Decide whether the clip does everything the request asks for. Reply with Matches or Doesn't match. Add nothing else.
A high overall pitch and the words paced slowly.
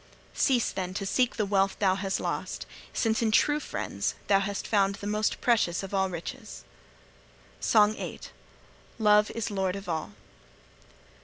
Doesn't match